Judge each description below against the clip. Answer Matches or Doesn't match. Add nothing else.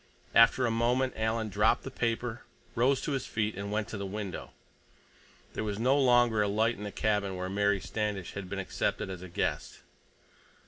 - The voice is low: Matches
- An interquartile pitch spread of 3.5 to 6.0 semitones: Doesn't match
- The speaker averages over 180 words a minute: Matches